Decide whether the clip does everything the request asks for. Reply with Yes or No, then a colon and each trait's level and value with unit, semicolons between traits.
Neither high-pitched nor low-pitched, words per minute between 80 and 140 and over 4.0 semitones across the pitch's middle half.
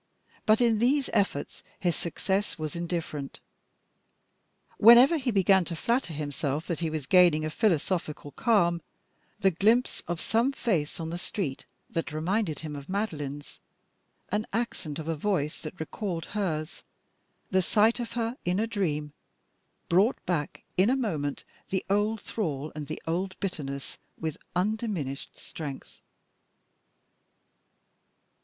Yes: medium, 175 Hz; slow, 135 wpm; wide, 5.6 semitones